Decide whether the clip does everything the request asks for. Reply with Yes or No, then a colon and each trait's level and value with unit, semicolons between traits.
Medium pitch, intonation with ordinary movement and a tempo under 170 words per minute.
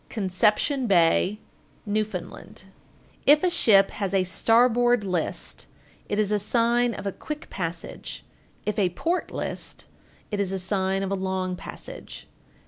No: high, 200 Hz; average, 3.8 semitones; average, 145 wpm